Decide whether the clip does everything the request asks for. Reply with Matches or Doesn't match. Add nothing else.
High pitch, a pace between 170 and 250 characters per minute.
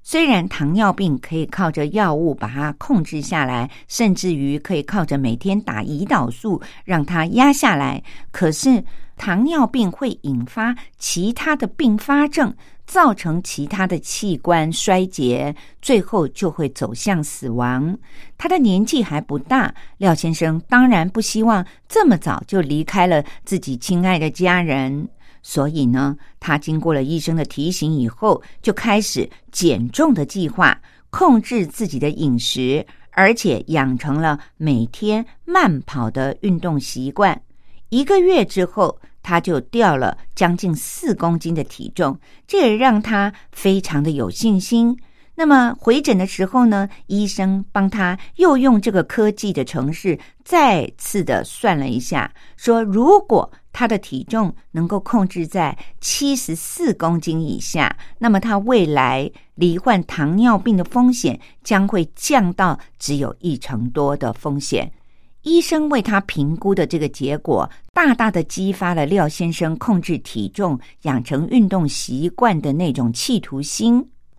Doesn't match